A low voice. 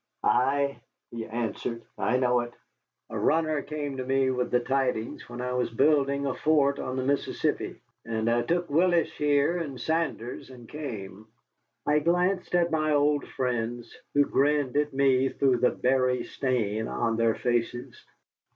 Yes: low, 130 Hz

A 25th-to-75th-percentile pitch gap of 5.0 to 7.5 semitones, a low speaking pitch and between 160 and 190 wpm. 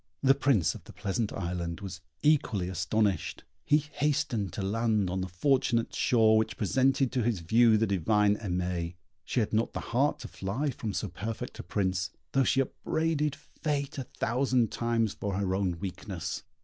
Yes: wide, 5.6 semitones; low, 110 Hz; average, 175 wpm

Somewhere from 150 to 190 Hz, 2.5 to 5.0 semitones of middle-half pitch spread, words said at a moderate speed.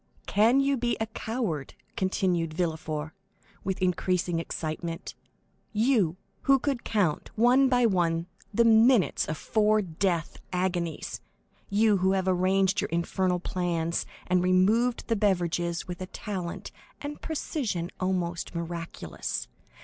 No: medium, 185 Hz; average, 4.4 semitones; slow, 125 wpm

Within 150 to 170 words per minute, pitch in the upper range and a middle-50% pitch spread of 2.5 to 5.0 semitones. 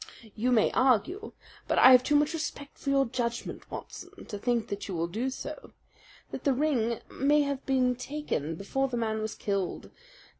No: average, 185 wpm; very high, 250 Hz; average, 4.2 semitones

